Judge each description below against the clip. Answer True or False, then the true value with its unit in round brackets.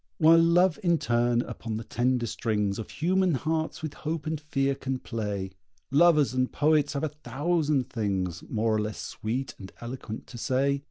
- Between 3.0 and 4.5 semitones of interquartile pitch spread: False (5.5 semitones)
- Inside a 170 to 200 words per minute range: True (175 wpm)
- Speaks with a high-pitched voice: False (135 Hz)